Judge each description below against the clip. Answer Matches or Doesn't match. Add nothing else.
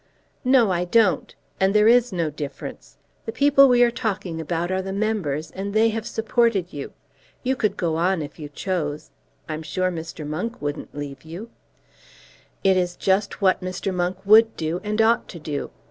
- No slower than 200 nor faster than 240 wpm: Doesn't match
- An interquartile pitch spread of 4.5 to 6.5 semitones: Matches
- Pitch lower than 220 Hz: Matches